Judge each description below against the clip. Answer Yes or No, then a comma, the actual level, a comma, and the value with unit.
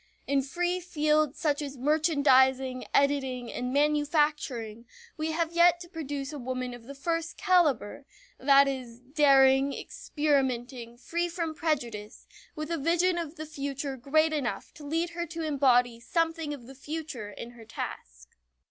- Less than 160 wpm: Yes, average, 150 wpm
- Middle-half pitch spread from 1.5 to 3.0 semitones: No, average, 3.7 semitones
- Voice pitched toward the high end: Yes, very high, 285 Hz